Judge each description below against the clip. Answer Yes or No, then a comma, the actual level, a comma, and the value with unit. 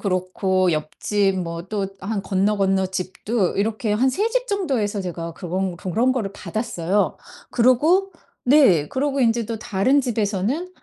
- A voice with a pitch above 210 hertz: No, high, 205 Hz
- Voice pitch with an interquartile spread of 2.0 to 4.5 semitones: No, average, 5.2 semitones